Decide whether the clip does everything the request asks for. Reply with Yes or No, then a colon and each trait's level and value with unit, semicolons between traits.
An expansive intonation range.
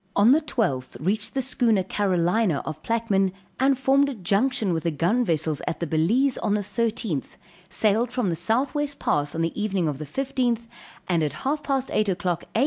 Yes: wide, 6.7 semitones